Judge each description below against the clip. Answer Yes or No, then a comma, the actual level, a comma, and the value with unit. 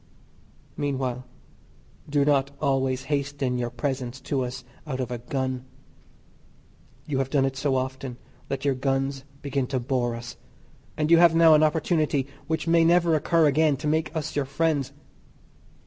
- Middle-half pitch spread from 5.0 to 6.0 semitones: No, average, 2.7 semitones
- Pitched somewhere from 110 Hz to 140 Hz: Yes, low, 135 Hz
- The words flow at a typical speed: Yes, average, 160 wpm